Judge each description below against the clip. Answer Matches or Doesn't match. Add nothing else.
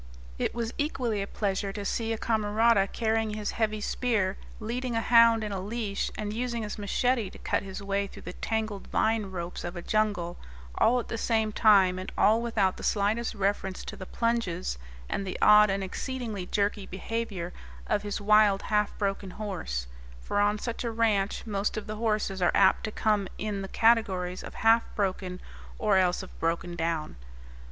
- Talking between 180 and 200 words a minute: Matches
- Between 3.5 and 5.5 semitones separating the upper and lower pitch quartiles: Doesn't match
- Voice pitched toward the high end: Matches